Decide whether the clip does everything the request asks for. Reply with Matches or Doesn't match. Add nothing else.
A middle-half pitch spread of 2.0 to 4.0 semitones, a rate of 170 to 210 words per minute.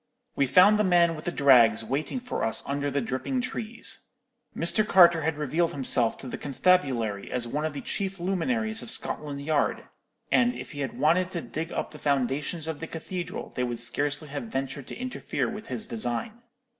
Doesn't match